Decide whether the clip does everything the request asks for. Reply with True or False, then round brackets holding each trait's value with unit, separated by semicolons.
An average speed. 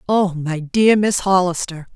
True (155 wpm)